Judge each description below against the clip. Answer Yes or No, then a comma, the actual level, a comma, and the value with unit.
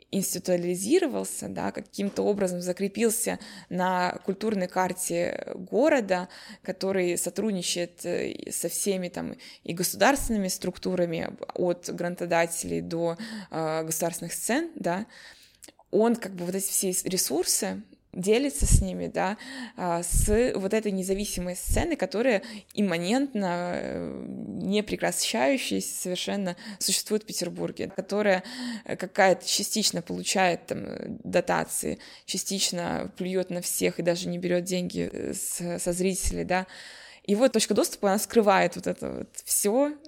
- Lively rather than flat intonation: No, average, 3.3 semitones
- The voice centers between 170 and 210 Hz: Yes, high, 190 Hz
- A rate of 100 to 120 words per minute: Yes, slow, 110 wpm